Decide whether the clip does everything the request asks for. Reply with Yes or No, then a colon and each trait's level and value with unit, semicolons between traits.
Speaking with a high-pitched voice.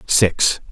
No: very low, 95 Hz